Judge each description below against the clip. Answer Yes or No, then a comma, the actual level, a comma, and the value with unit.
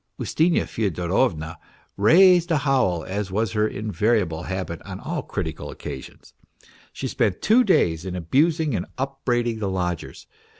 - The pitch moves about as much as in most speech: No, wide, 7.4 semitones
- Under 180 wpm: Yes, average, 140 wpm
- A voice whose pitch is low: Yes, low, 105 Hz